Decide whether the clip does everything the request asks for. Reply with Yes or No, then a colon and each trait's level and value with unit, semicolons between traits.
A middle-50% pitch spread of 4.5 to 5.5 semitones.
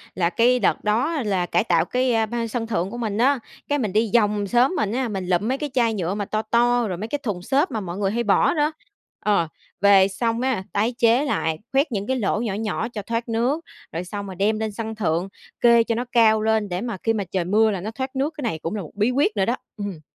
No: average, 3.3 semitones